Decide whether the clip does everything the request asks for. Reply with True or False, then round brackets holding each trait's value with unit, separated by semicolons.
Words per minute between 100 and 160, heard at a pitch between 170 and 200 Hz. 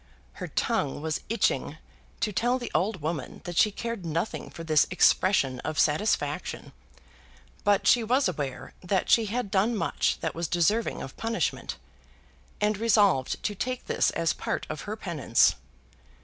True (155 wpm; 190 Hz)